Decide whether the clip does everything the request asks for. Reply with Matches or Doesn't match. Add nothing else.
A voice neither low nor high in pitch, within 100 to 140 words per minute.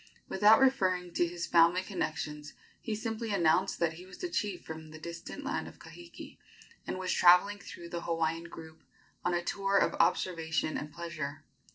Doesn't match